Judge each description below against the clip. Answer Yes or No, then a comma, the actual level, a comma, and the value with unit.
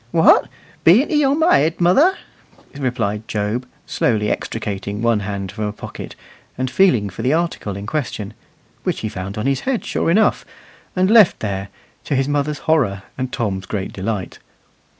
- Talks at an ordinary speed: Yes, average, 170 wpm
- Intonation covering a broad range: Yes, wide, 7.8 semitones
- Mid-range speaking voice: No, low, 120 Hz